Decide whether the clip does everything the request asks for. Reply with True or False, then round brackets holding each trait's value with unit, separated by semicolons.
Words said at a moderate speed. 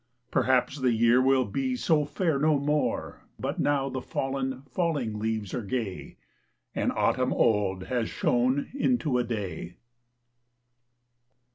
False (130 wpm)